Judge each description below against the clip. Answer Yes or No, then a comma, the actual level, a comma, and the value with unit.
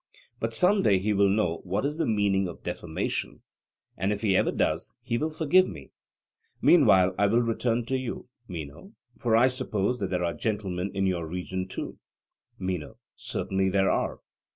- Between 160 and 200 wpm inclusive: Yes, average, 175 wpm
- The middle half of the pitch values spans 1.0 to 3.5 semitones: No, average, 4.0 semitones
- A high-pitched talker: No, low, 100 Hz